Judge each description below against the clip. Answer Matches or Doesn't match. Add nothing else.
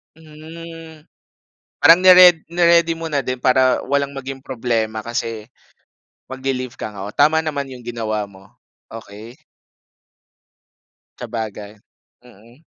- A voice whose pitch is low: Matches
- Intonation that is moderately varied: Doesn't match